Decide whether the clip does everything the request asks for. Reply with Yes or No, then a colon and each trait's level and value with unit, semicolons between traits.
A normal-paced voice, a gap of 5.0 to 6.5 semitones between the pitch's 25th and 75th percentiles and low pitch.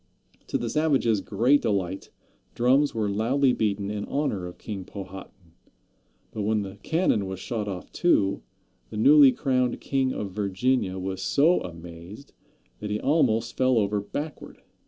Yes: average, 150 wpm; average, 5.3 semitones; low, 105 Hz